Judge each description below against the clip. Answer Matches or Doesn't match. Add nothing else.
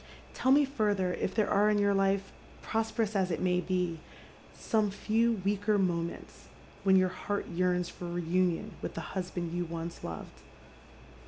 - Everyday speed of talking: Matches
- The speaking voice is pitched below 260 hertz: Matches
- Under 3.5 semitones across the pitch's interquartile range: Matches